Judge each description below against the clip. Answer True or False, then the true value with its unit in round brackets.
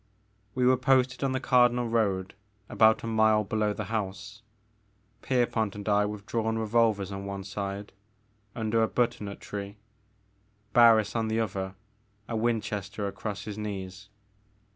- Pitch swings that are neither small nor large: False (2.3 semitones)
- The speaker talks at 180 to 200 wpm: False (140 wpm)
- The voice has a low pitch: True (110 Hz)